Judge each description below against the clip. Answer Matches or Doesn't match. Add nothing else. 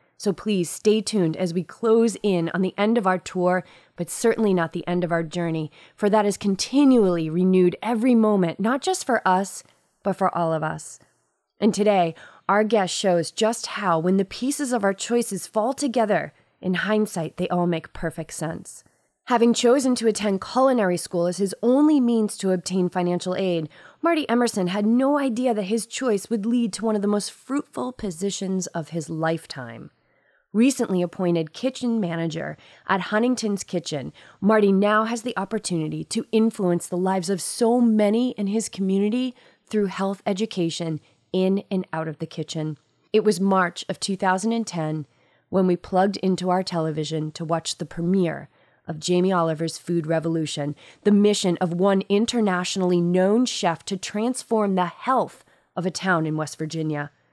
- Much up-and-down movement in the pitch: Doesn't match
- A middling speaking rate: Matches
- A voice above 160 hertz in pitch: Matches